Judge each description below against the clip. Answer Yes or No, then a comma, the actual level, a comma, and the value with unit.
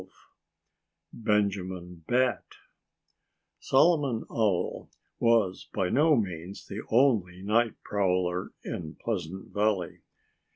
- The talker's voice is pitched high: No, low, 100 Hz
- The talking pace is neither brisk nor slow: No, slow, 90 wpm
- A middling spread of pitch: Yes, average, 4.2 semitones